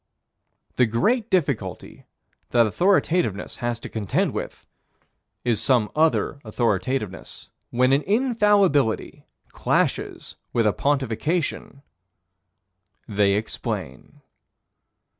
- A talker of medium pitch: No, low, 130 Hz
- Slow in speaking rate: Yes, slow, 85 wpm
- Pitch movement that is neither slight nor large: No, wide, 7.3 semitones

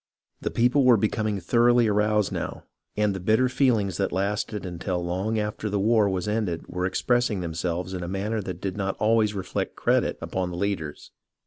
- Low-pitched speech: Yes, low, 100 Hz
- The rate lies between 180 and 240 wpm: Yes, average, 185 wpm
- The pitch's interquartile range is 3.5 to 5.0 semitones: No, average, 3.0 semitones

